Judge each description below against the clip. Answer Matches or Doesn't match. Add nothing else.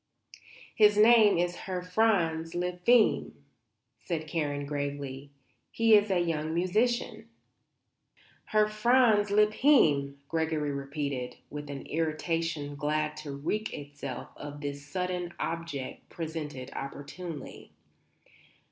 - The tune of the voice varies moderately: Doesn't match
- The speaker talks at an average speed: Doesn't match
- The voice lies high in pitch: Doesn't match